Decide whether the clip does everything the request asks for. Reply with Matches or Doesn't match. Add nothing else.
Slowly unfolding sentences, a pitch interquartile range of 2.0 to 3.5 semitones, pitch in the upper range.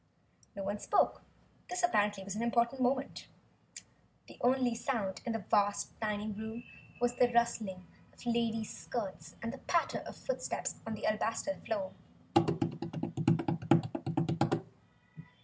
Matches